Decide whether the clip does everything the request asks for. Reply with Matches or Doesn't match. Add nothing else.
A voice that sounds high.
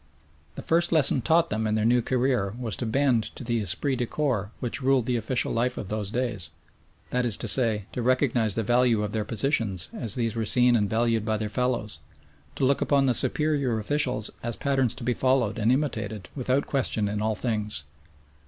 Doesn't match